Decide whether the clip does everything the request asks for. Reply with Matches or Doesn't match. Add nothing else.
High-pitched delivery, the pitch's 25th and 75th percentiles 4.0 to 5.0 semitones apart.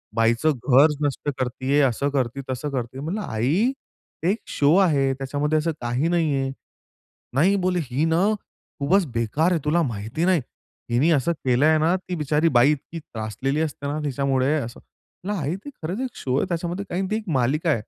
Doesn't match